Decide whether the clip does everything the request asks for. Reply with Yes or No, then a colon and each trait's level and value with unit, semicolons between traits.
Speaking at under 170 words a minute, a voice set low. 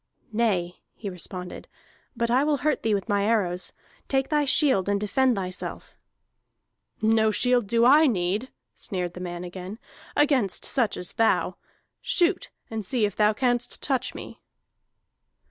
No: average, 145 wpm; high, 220 Hz